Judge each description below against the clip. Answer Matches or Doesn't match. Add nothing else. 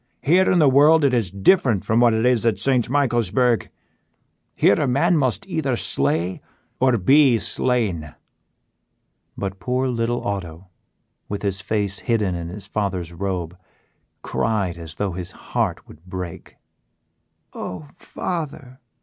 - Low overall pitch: Matches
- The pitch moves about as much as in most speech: Doesn't match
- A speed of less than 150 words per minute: Matches